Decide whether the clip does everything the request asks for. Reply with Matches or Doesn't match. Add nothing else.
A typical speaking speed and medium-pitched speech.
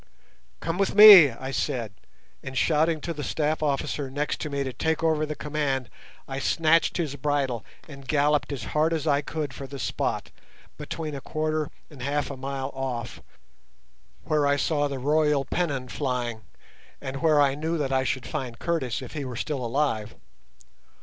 Matches